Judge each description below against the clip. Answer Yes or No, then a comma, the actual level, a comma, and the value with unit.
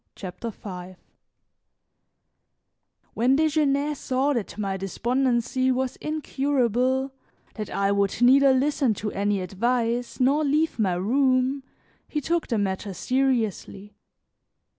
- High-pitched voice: Yes, very high, 250 Hz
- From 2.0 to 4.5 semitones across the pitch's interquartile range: No, average, 4.9 semitones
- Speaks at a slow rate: Yes, slow, 110 wpm